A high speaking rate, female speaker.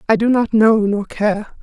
Yes: fast, 220 wpm; female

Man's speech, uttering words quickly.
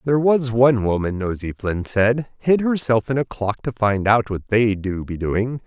Yes: male; fast, 210 wpm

